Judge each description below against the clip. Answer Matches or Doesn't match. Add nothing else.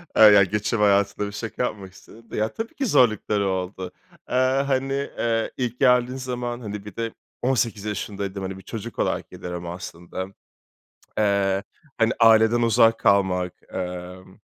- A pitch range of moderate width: Matches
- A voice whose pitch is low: Matches